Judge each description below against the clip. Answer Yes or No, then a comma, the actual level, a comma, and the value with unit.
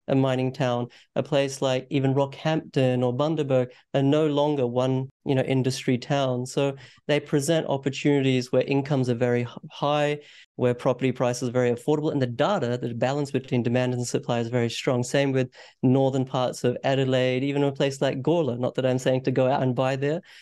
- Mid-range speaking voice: No, low, 130 Hz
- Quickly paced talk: No, average, 195 wpm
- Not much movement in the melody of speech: Yes, narrow, 2.0 semitones